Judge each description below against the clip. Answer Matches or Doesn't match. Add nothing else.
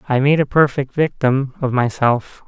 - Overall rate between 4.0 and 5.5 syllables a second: Matches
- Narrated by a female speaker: Doesn't match